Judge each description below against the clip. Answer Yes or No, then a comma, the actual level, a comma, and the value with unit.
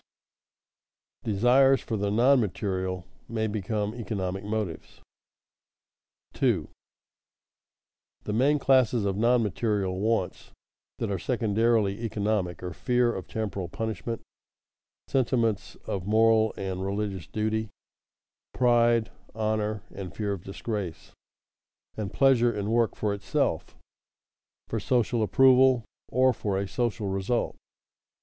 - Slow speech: Yes, slow, 115 wpm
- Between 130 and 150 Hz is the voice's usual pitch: No, low, 110 Hz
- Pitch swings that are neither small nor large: Yes, average, 3.0 semitones